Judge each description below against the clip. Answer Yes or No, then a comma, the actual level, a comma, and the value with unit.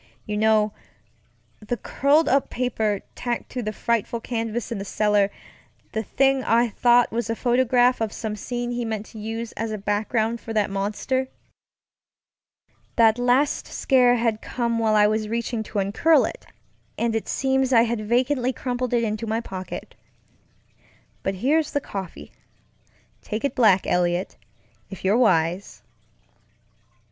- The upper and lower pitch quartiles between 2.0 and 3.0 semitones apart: Yes, narrow, 2.6 semitones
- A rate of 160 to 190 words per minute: No, average, 150 wpm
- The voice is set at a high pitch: Yes, high, 230 Hz